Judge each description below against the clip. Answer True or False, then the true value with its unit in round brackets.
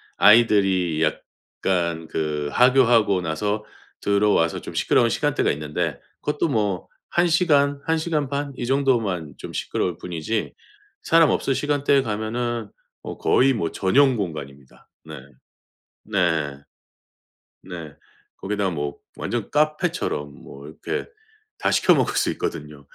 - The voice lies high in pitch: False (105 Hz)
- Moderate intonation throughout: False (8.8 semitones)